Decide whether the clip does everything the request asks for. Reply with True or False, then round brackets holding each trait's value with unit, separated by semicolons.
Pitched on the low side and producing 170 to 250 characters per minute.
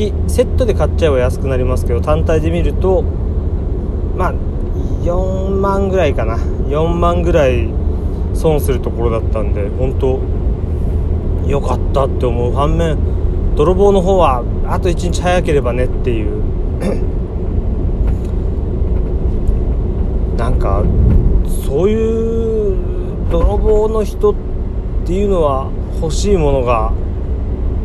True (85 Hz; 215 characters per minute)